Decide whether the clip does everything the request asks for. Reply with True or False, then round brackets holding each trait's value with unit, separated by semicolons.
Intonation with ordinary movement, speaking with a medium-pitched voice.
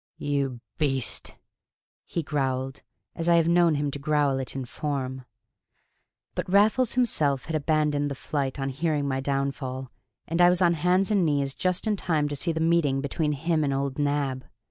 True (3.5 semitones; 145 Hz)